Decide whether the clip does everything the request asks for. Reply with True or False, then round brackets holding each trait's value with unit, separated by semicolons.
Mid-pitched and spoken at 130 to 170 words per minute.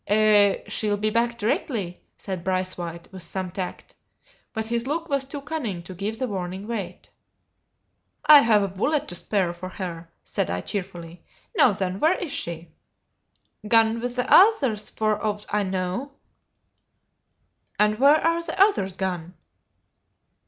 False (210 Hz; 145 wpm)